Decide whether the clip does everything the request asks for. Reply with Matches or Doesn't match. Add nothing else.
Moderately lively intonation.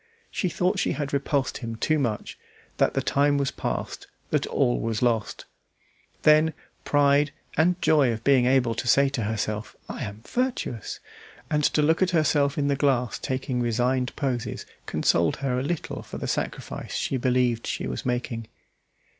Matches